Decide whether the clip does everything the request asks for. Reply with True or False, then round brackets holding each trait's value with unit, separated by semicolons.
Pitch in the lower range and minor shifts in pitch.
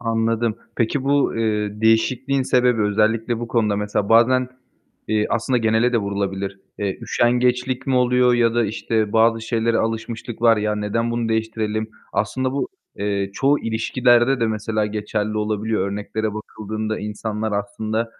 True (110 Hz; 2.0 semitones)